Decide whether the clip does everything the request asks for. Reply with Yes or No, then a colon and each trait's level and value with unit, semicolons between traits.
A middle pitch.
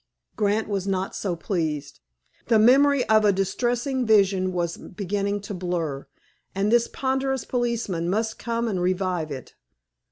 No: high, 200 Hz